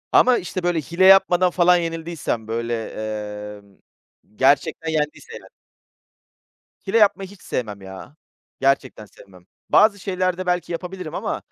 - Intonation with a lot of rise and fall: Yes, wide, 5.8 semitones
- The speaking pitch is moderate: Yes, medium, 170 Hz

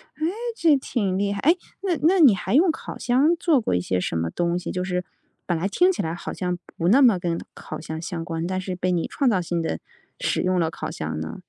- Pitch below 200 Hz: Yes, medium, 185 Hz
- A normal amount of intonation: No, wide, 7.8 semitones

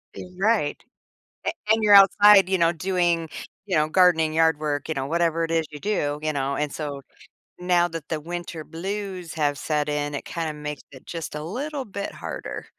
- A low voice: No, medium, 165 Hz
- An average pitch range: Yes, average, 3.5 semitones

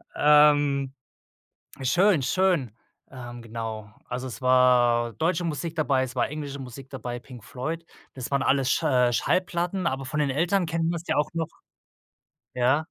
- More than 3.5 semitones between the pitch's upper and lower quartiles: Yes, average, 4.4 semitones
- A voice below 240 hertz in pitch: Yes, low, 135 Hz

